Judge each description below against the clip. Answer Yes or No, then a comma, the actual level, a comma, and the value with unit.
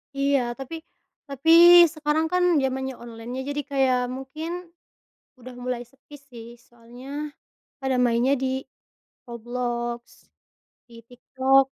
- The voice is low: No, very high, 260 Hz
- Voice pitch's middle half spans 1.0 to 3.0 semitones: Yes, narrow, 2.5 semitones